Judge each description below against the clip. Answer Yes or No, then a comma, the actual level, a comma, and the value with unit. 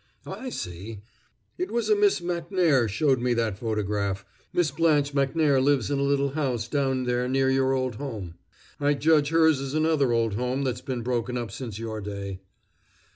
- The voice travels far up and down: No, average, 4.2 semitones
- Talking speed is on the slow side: No, average, 180 wpm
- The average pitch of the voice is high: No, low, 130 Hz